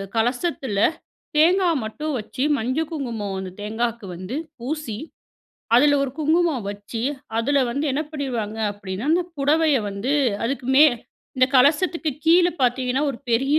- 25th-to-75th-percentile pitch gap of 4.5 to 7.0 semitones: Yes, average, 5.1 semitones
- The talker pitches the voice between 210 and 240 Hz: No, very high, 260 Hz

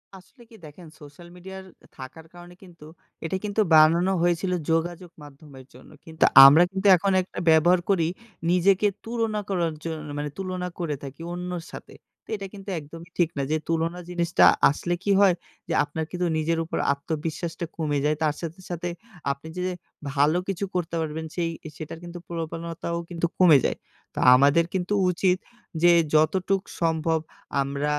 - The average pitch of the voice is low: No, medium, 170 Hz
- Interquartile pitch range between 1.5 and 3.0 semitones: Yes, narrow, 2.5 semitones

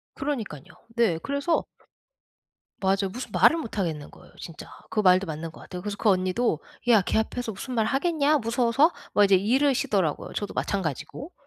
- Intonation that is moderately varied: No, wide, 6.0 semitones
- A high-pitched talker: Yes, high, 215 Hz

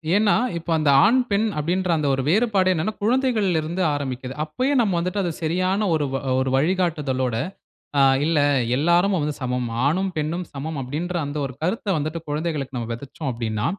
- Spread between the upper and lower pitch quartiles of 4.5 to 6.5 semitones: Yes, average, 4.9 semitones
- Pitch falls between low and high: Yes, medium, 160 Hz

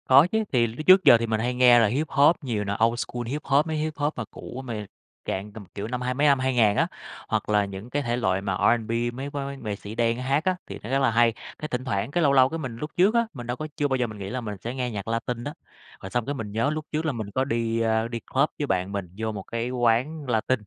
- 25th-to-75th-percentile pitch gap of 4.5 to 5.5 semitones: No, average, 3.9 semitones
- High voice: No, low, 120 Hz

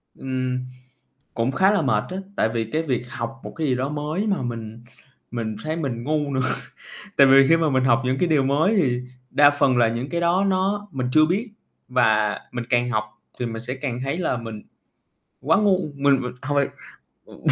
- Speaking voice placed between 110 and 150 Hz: Yes, low, 135 Hz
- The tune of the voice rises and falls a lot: No, average, 4.4 semitones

